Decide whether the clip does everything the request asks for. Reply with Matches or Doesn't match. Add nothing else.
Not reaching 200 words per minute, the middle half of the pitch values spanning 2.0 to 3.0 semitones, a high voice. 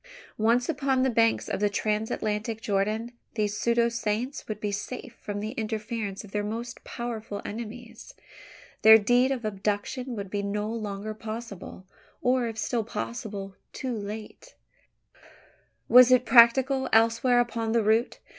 Matches